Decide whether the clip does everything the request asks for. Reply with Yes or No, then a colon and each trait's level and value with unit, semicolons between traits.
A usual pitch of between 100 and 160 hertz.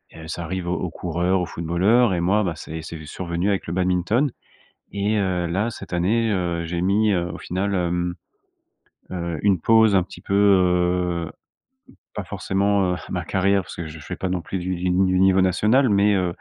No: very low, 90 Hz